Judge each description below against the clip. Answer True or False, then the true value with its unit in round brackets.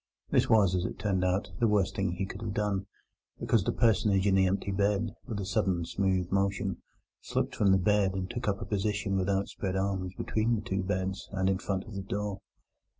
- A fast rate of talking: True (215 wpm)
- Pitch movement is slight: True (1.5 semitones)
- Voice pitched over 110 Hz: False (100 Hz)